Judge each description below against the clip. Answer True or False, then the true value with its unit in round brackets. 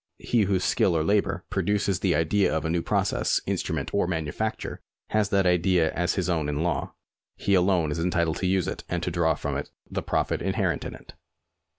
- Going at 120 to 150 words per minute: False (205 wpm)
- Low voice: True (90 Hz)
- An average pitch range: True (3.0 semitones)